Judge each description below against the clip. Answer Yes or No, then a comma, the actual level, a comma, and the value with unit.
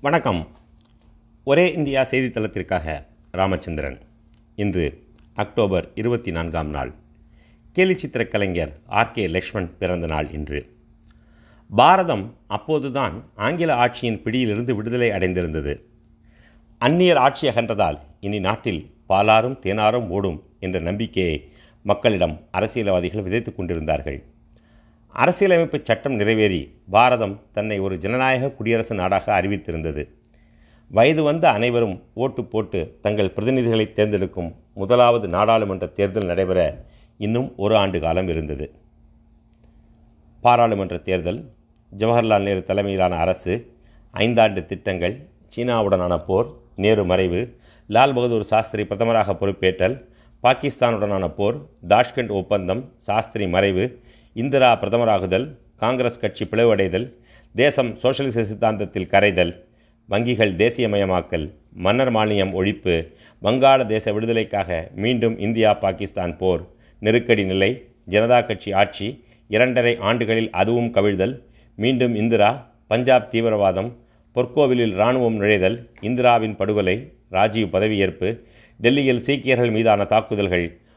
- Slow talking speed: No, average, 100 wpm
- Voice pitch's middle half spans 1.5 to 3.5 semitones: No, average, 4.2 semitones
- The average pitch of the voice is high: No, low, 110 Hz